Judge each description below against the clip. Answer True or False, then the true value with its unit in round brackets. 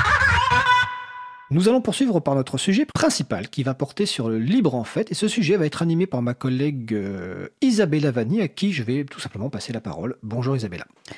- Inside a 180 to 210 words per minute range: True (200 wpm)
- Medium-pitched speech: True (150 Hz)